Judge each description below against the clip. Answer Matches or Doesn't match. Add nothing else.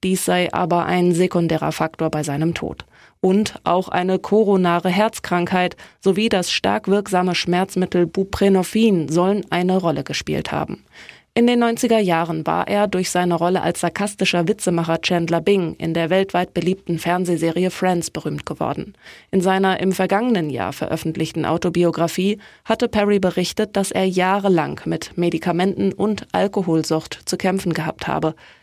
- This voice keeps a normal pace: Matches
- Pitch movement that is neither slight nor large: Doesn't match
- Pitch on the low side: Doesn't match